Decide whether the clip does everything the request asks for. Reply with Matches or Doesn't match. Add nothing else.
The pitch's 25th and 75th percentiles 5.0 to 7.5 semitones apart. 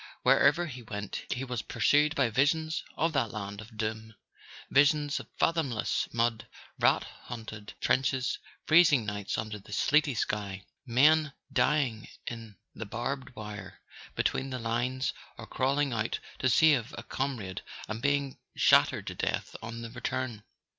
Doesn't match